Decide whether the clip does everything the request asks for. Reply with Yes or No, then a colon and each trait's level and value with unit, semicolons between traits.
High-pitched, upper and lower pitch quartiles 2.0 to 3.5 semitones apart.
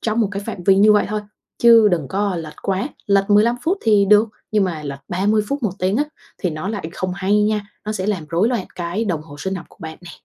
Yes: high, 200 Hz; average, 3.2 semitones